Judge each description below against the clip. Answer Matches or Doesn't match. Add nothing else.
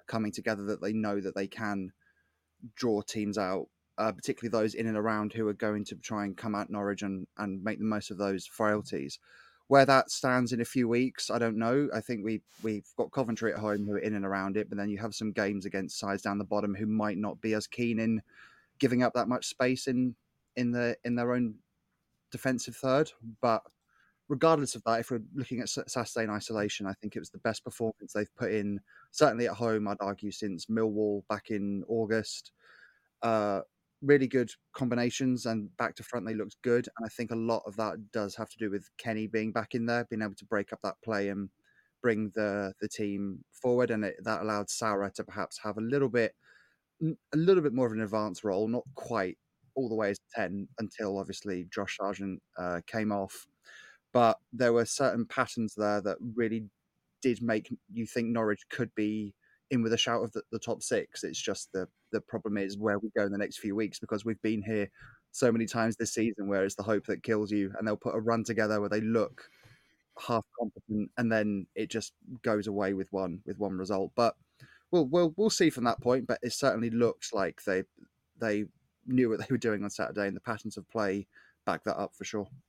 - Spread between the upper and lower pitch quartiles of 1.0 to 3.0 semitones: Matches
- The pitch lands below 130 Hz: Matches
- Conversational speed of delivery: Doesn't match